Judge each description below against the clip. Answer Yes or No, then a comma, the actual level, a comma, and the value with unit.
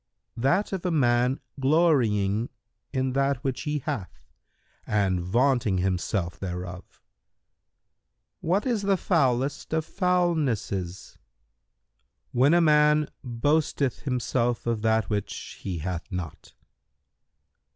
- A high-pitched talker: No, low, 125 Hz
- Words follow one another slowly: Yes, slow, 105 wpm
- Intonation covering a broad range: Yes, wide, 7.4 semitones